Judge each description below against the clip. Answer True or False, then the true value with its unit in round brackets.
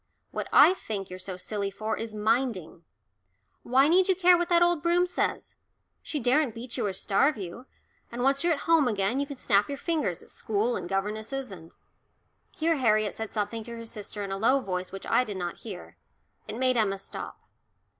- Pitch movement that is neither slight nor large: False (5.7 semitones)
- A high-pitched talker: True (225 Hz)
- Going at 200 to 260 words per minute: True (205 wpm)